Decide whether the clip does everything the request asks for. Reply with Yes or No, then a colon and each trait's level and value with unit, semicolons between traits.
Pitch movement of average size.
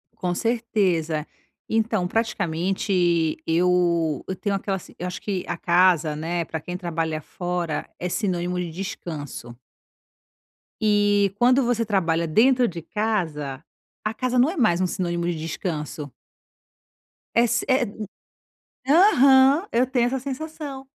No: wide, 5.8 semitones